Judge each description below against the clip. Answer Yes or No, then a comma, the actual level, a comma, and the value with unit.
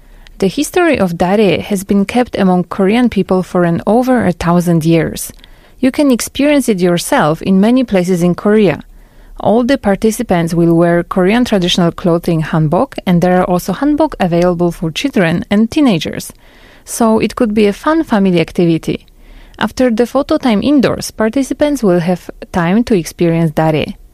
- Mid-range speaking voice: No, high, 195 Hz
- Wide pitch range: Yes, wide, 5.7 semitones